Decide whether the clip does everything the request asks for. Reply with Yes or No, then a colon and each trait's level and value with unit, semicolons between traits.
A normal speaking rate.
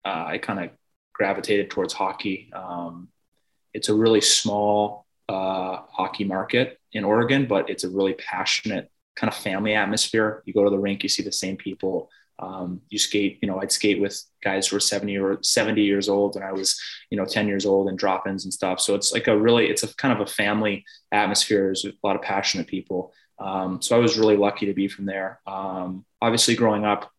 No: fast, 210 wpm